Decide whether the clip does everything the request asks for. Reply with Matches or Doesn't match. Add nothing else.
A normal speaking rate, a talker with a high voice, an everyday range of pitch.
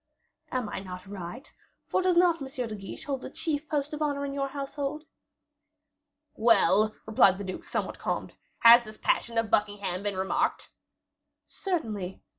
Doesn't match